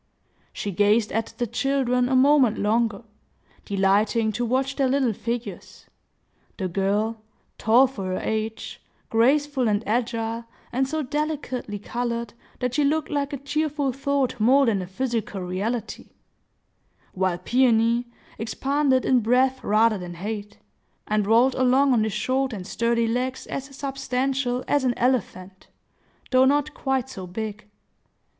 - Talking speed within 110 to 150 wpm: Yes, slow, 135 wpm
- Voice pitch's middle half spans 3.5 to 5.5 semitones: Yes, average, 3.8 semitones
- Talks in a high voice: Yes, high, 240 Hz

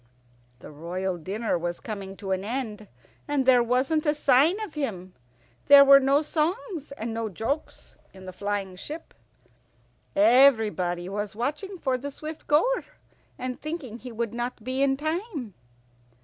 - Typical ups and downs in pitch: No, wide, 6.2 semitones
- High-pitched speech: Yes, very high, 250 Hz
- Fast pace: No, average, 150 wpm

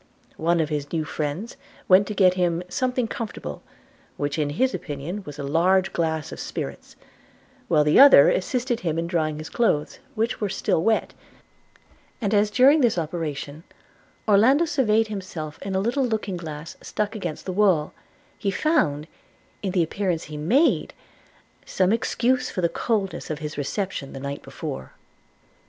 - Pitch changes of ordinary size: No, wide, 5.9 semitones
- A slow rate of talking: No, average, 160 wpm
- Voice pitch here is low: No, medium, 185 Hz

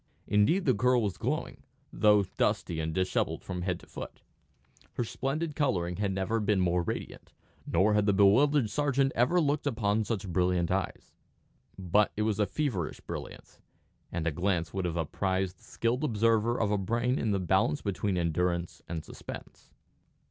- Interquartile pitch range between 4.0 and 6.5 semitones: Yes, average, 4.7 semitones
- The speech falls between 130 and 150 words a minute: No, average, 170 wpm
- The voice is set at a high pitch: No, low, 100 Hz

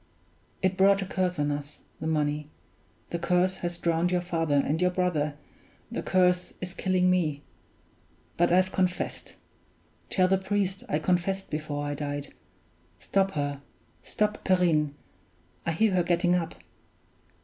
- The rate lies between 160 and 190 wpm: No, average, 145 wpm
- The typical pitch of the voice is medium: Yes, medium, 175 Hz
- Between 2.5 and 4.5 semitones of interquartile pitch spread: Yes, average, 3.5 semitones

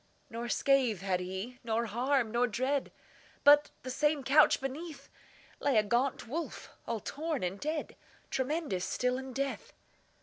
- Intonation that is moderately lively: Yes, average, 3.8 semitones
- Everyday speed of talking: No, slow, 130 wpm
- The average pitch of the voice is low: No, very high, 255 Hz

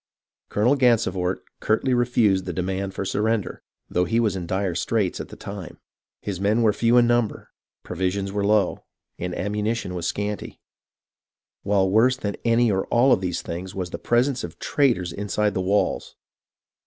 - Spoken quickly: No, average, 175 wpm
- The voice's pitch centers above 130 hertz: No, low, 100 Hz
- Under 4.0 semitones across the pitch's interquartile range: Yes, average, 3.6 semitones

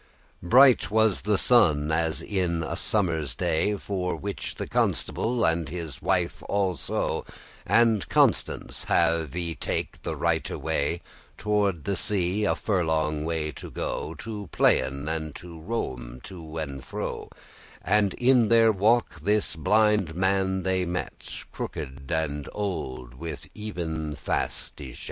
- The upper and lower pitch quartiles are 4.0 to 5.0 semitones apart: Yes, average, 4.7 semitones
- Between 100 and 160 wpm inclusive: Yes, average, 140 wpm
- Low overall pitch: Yes, very low, 85 Hz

